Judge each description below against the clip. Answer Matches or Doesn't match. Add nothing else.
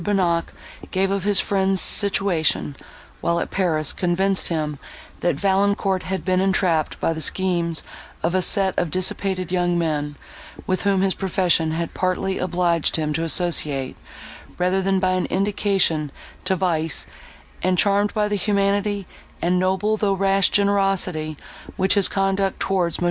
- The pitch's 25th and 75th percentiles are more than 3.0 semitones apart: Doesn't match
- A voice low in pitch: Doesn't match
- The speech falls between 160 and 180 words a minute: Doesn't match